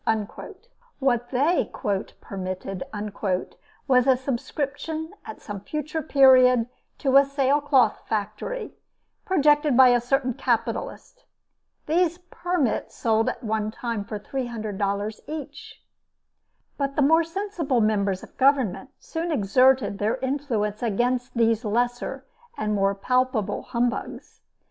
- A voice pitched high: Yes, very high, 250 Hz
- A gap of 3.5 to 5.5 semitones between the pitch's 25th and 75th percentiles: Yes, average, 4.7 semitones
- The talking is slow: Yes, slow, 110 wpm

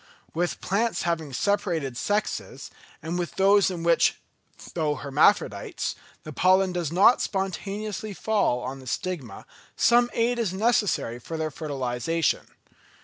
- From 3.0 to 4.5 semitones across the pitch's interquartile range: No, average, 5.3 semitones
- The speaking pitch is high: No, medium, 175 Hz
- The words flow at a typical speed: No, slow, 130 wpm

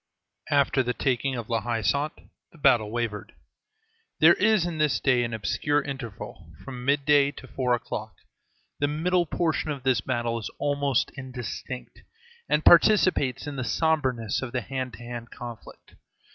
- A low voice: Yes, low, 130 Hz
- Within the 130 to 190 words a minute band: Yes, average, 160 wpm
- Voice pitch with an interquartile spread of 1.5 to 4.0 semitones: Yes, average, 3.6 semitones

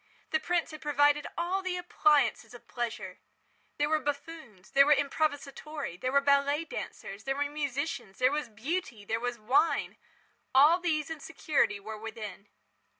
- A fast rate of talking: No, average, 155 wpm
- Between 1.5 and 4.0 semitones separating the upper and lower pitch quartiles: No, average, 4.5 semitones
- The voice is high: Yes, very high, 285 Hz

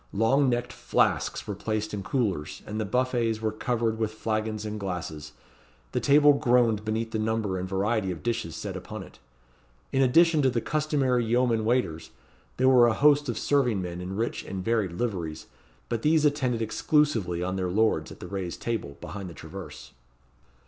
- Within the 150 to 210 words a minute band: Yes, average, 180 wpm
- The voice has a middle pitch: No, low, 110 Hz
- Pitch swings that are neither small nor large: Yes, average, 4.5 semitones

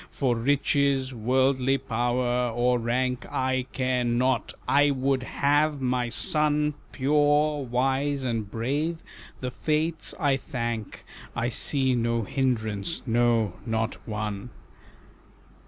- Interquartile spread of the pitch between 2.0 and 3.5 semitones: Yes, average, 2.9 semitones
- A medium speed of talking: No, slow, 110 wpm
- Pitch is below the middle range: Yes, low, 130 Hz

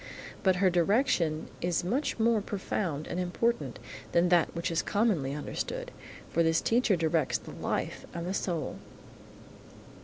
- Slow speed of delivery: No, average, 145 wpm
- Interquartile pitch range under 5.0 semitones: Yes, average, 3.8 semitones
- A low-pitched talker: No, medium, 175 Hz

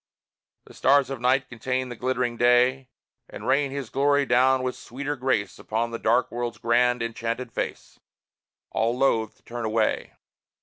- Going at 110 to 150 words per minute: No, average, 160 wpm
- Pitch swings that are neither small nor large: No, narrow, 2.0 semitones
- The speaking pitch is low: Yes, low, 125 Hz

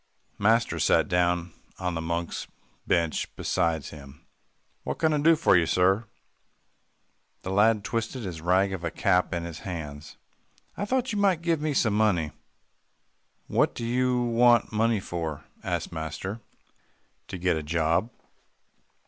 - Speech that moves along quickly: No, average, 150 wpm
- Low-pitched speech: Yes, very low, 95 Hz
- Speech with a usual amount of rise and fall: No, wide, 5.8 semitones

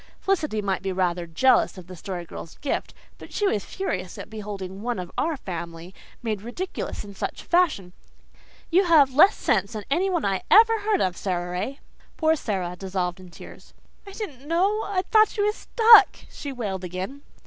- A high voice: Yes, high, 215 Hz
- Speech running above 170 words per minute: Yes, average, 185 wpm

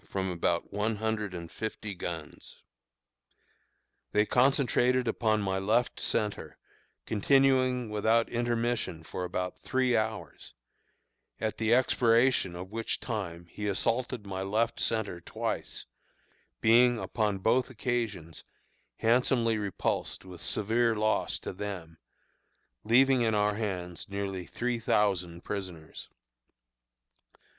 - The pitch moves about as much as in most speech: Yes, average, 3.8 semitones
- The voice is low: Yes, low, 110 Hz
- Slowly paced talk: Yes, slow, 110 wpm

